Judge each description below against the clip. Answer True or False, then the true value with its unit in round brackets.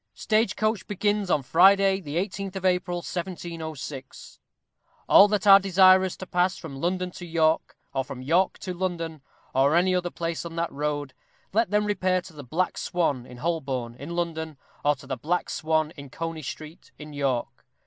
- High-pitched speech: False (170 Hz)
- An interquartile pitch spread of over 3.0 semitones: True (3.9 semitones)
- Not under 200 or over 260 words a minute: False (180 wpm)